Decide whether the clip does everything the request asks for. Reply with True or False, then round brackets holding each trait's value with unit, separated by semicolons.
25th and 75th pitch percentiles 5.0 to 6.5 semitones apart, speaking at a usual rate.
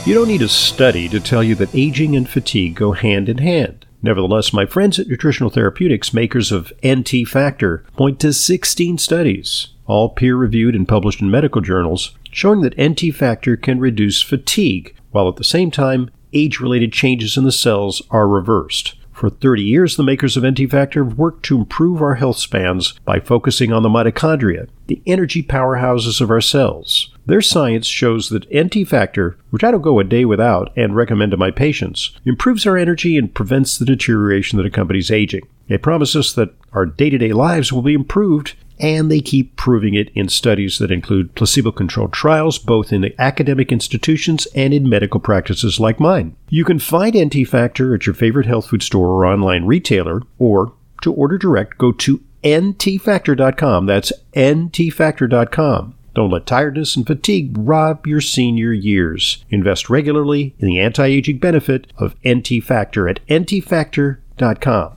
True (5.4 semitones; 175 wpm)